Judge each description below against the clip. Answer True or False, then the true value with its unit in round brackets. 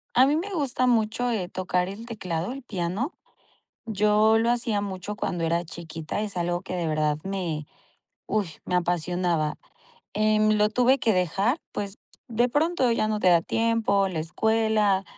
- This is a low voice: False (205 Hz)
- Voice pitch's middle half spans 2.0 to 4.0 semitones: False (4.4 semitones)